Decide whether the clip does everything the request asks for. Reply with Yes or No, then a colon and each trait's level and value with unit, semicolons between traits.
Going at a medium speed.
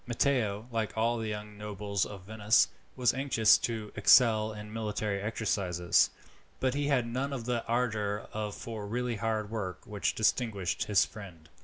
Yes: average, 155 wpm